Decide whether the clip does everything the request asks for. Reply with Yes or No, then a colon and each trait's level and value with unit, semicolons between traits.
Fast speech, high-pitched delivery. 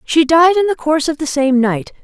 Yes: fast, 265 wpm; very high, 300 Hz